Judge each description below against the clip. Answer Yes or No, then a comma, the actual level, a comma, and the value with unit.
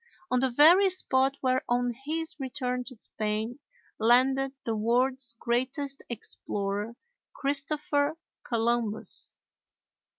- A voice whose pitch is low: No, very high, 255 Hz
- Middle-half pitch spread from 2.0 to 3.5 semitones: Yes, average, 2.9 semitones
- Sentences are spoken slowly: Yes, slow, 100 wpm